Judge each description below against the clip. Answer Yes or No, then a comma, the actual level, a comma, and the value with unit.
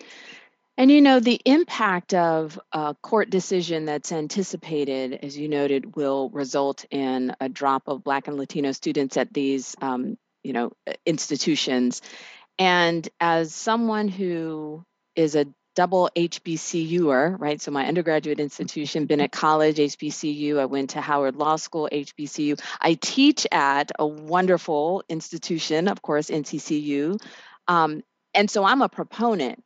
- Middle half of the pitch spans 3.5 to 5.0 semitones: Yes, average, 3.8 semitones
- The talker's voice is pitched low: No, medium, 155 Hz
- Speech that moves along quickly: No, average, 140 wpm